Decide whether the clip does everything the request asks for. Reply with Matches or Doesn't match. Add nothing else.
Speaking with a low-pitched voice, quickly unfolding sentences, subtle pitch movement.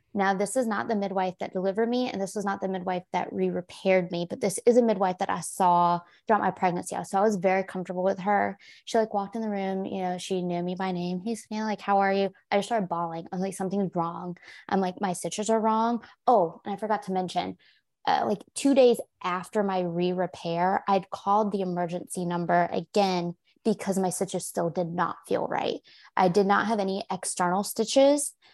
Doesn't match